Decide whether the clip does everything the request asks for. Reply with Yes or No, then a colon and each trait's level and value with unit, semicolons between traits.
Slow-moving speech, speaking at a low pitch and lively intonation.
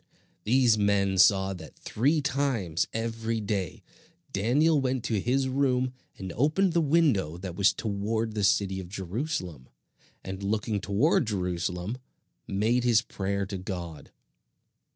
No: slow, 130 wpm; low, 105 Hz; average, 4.8 semitones